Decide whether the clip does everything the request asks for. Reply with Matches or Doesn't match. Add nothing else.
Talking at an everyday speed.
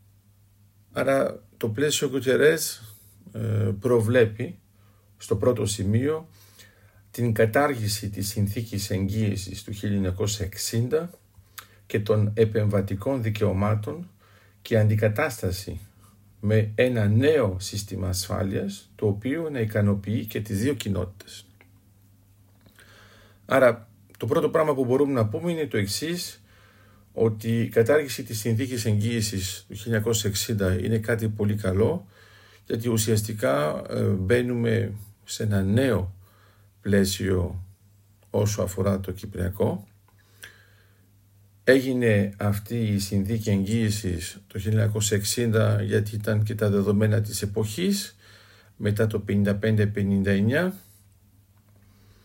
Doesn't match